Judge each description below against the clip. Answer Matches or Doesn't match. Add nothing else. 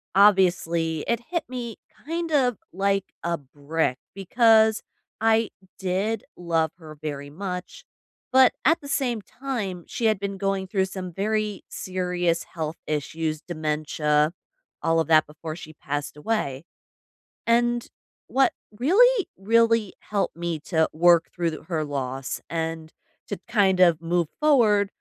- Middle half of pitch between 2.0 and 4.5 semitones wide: Doesn't match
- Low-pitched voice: Doesn't match